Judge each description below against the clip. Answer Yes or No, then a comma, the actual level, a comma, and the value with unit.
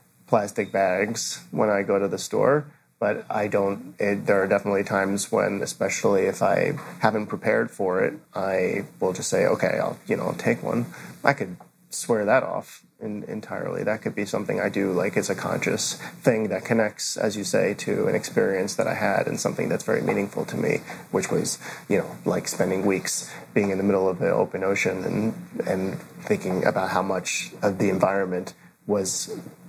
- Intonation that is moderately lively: No, narrow, 1.0 semitones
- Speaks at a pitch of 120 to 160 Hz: No, low, 100 Hz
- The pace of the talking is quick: No, average, 195 wpm